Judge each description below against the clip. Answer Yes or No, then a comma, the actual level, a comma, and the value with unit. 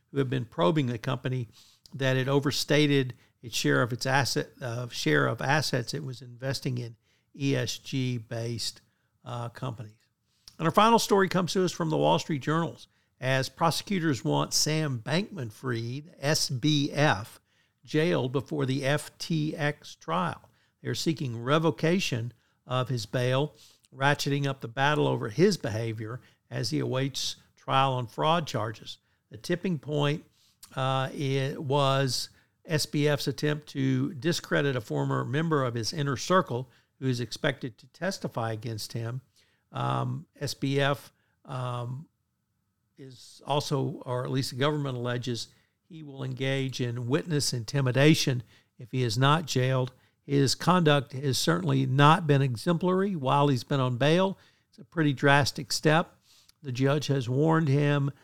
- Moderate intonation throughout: Yes, average, 3.4 semitones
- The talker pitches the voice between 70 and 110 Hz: No, low, 135 Hz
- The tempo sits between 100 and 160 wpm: Yes, average, 140 wpm